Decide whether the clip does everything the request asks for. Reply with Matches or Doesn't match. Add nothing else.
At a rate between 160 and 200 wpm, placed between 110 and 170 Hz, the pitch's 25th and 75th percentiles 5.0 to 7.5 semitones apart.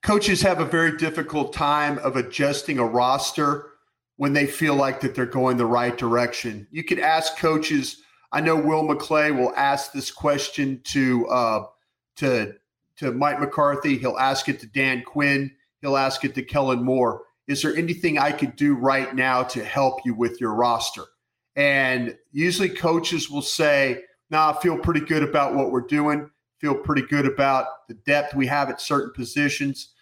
Doesn't match